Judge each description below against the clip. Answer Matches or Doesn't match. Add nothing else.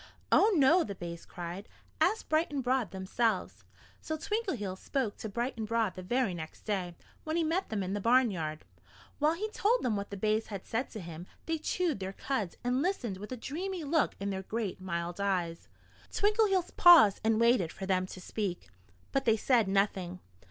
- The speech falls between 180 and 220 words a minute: Matches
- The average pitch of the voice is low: Doesn't match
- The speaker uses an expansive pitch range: Matches